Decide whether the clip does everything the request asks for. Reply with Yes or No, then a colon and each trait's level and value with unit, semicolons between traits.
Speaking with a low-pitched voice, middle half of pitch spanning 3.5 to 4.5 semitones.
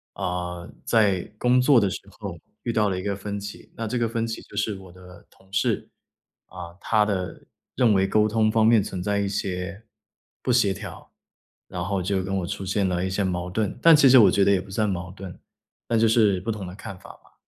No: low, 100 Hz; average, 2.9 semitones